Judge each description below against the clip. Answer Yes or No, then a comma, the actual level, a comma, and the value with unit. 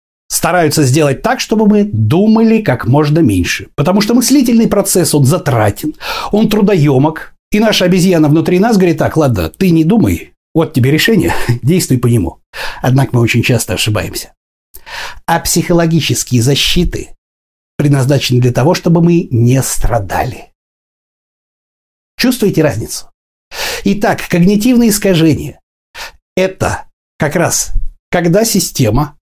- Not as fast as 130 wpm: Yes, average, 120 wpm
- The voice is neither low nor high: Yes, medium, 160 Hz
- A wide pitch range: Yes, wide, 7.2 semitones